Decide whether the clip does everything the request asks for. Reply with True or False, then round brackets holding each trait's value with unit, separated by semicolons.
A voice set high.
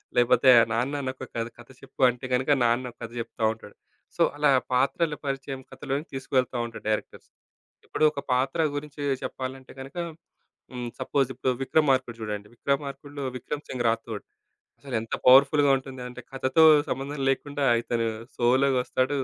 False (130 Hz)